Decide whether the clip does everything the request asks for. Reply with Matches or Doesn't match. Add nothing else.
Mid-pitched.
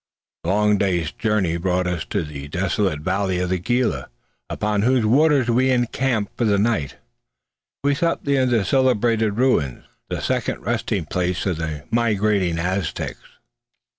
Doesn't match